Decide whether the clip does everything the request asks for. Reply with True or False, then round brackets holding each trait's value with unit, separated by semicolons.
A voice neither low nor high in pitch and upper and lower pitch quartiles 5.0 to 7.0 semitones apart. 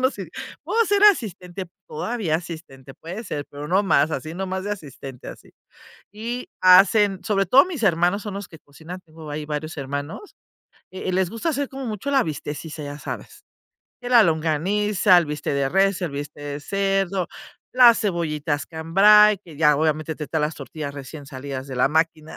True (170 Hz; 5.3 semitones)